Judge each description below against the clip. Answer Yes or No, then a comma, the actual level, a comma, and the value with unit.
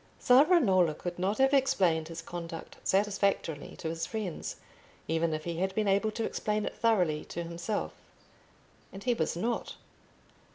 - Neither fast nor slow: Yes, average, 155 wpm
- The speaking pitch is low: No, high, 190 Hz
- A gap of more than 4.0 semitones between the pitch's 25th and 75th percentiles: Yes, average, 4.6 semitones